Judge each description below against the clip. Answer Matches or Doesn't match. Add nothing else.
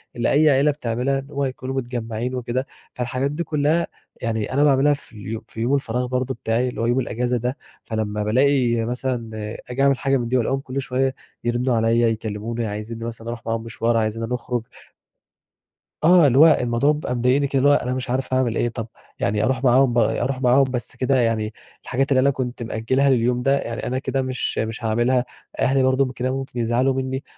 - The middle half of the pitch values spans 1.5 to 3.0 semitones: Matches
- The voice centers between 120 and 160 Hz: Matches